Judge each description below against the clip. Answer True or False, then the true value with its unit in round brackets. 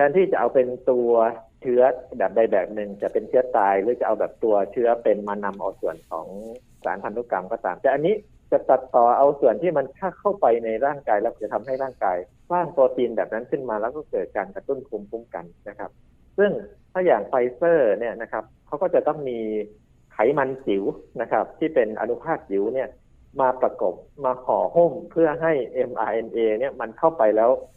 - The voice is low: True (125 Hz)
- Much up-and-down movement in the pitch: True (6.4 semitones)